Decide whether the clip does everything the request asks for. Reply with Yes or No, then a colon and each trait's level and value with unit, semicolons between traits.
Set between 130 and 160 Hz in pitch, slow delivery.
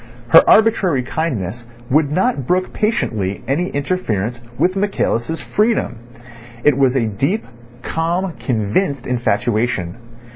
Yes: medium, 140 Hz; slow, 110 wpm